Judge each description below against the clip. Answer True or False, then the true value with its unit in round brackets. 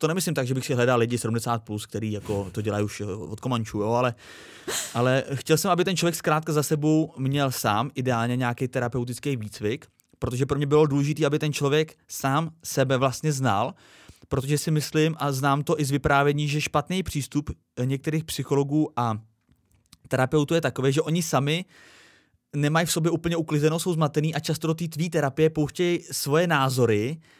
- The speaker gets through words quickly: True (180 wpm)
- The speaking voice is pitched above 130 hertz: True (140 Hz)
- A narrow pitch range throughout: False (3.9 semitones)